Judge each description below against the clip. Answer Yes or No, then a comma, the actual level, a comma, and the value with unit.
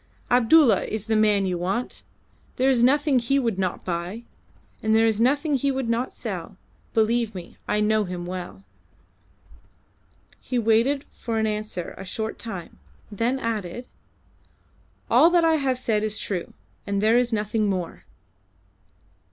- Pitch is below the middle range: No, high, 220 Hz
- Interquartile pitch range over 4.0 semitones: No, average, 3.7 semitones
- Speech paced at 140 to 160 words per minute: Yes, average, 150 wpm